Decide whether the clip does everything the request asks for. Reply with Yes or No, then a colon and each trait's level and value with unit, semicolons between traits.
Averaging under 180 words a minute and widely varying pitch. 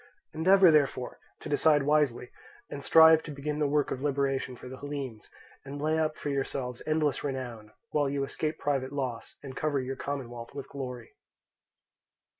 No: average, 165 wpm; narrow, 2.4 semitones